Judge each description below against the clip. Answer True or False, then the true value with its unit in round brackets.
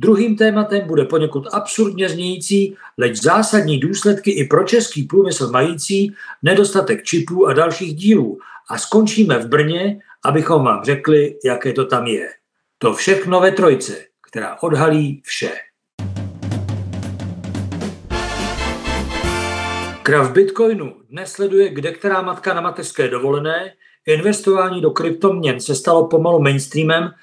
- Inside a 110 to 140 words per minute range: True (120 wpm)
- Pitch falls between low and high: True (170 Hz)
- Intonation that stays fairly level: False (5.6 semitones)